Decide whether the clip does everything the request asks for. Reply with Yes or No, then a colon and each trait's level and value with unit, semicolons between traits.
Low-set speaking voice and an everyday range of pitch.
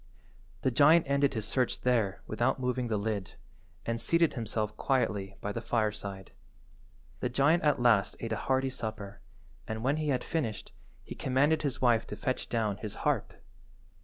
Yes: low, 120 Hz; average, 3.8 semitones